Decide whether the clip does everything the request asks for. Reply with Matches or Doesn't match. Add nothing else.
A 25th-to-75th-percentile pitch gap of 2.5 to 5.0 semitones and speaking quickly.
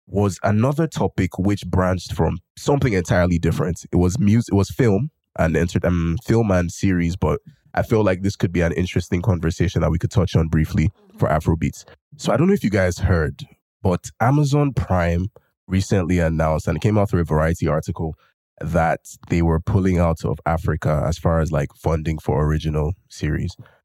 Doesn't match